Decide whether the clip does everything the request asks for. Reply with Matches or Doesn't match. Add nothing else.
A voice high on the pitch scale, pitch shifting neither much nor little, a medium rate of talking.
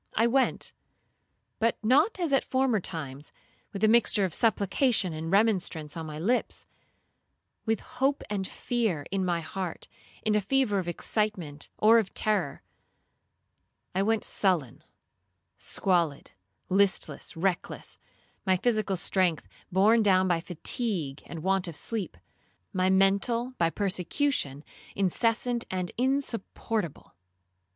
Doesn't match